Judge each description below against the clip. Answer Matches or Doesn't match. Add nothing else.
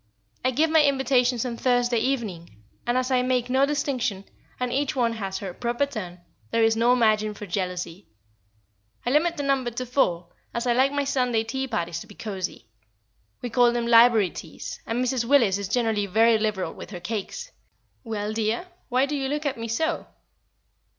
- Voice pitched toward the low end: Doesn't match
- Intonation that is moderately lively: Matches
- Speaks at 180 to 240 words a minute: Matches